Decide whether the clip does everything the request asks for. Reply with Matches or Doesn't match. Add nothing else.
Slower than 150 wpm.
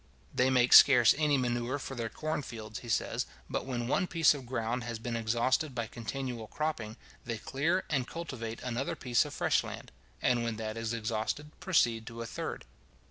Doesn't match